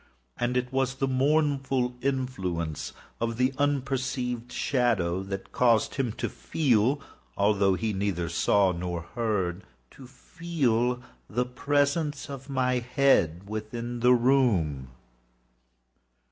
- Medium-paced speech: No, slow, 105 wpm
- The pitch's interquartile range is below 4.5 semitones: No, average, 5.1 semitones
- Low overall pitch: Yes, low, 125 Hz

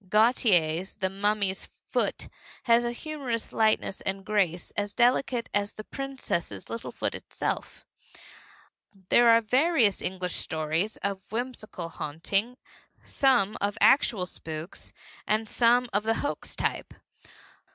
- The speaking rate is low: Yes, slow, 130 wpm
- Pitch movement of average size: Yes, average, 4.0 semitones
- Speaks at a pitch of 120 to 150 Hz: No, high, 215 Hz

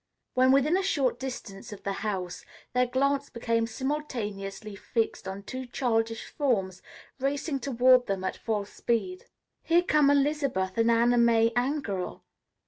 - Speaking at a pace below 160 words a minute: Yes, average, 140 wpm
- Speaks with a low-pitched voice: No, high, 240 Hz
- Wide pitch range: No, average, 4.8 semitones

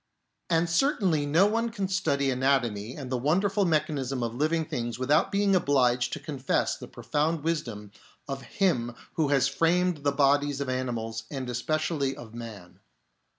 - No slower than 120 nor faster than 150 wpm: No, average, 160 wpm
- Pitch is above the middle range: No, medium, 140 Hz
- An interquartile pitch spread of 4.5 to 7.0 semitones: Yes, average, 4.8 semitones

